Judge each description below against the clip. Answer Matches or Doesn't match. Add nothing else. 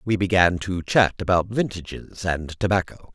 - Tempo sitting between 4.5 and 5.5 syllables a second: Matches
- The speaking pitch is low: Matches